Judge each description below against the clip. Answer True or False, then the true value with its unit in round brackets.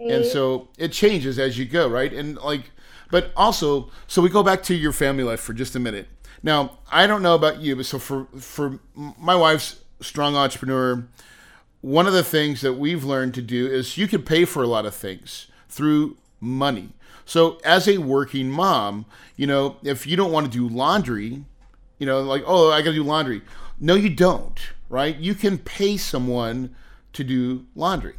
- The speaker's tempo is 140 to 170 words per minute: False (195 wpm)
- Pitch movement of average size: True (4.3 semitones)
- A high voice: False (140 Hz)